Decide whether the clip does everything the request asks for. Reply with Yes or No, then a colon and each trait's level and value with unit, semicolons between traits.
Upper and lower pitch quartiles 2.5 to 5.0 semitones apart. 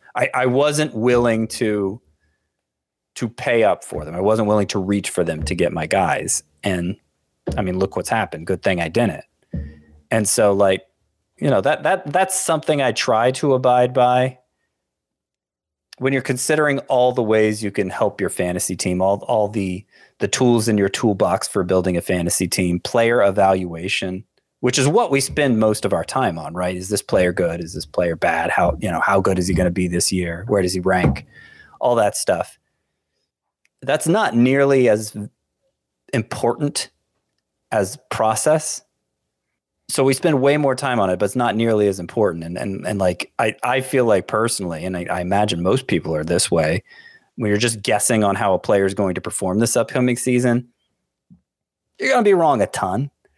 No: wide, 5.4 semitones